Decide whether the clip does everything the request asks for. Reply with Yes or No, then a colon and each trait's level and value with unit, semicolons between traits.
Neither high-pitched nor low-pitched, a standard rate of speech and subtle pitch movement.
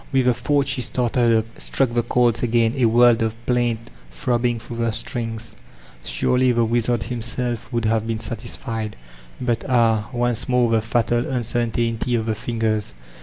No: low, 115 Hz; average, 165 wpm; narrow, 1.4 semitones